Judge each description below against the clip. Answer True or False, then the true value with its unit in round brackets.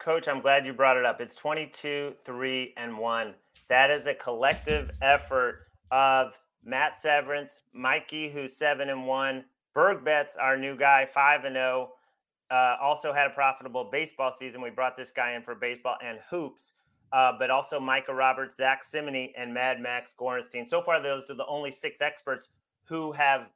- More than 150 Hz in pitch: False (135 Hz)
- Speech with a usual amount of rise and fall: False (2.0 semitones)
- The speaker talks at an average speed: True (180 wpm)